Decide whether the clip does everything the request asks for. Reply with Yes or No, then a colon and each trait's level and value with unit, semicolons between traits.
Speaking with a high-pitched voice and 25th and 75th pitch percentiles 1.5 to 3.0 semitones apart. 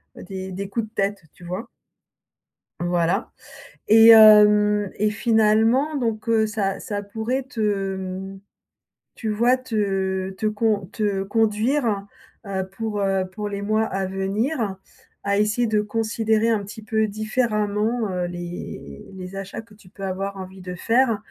Yes: high, 210 Hz; narrow, 2.4 semitones